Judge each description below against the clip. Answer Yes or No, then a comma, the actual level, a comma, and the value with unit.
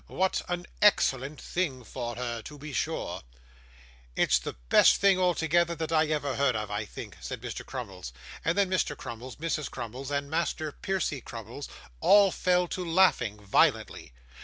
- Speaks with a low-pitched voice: No, medium, 150 Hz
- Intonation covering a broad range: Yes, wide, 6.1 semitones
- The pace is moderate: Yes, average, 160 wpm